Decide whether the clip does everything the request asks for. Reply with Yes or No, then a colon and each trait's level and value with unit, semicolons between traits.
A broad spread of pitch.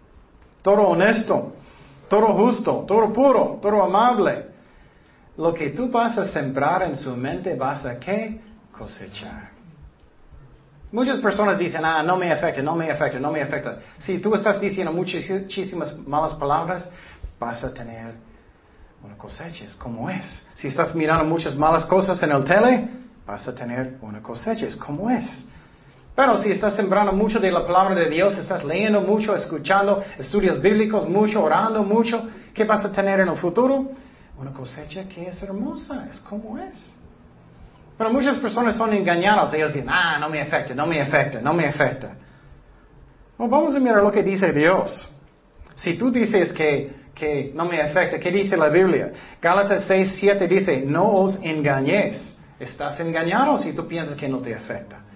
Yes: wide, 5.7 semitones